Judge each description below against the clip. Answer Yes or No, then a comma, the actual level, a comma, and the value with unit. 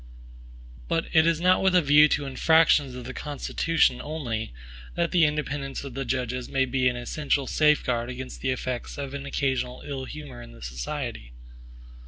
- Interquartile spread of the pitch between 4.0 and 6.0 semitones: No, average, 3.2 semitones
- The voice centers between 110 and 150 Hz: Yes, low, 135 Hz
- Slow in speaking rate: No, average, 170 wpm